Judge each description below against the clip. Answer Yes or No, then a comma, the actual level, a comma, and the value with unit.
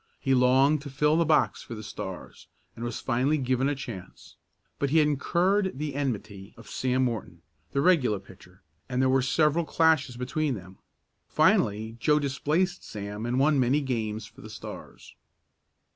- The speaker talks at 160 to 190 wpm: Yes, average, 170 wpm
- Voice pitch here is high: No, low, 130 Hz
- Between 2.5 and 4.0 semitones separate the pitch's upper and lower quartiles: No, average, 4.8 semitones